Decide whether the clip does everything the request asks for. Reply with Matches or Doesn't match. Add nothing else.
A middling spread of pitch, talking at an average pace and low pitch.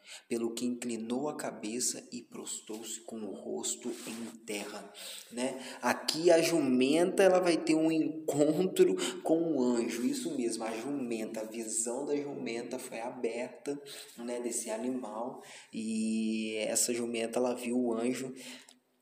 Matches